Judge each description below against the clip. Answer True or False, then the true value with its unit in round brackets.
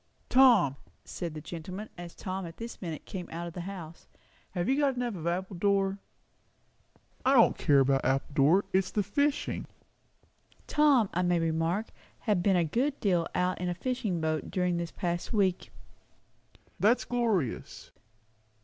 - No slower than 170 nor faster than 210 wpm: False (155 wpm)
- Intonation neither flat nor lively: True (4.1 semitones)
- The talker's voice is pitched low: False (180 Hz)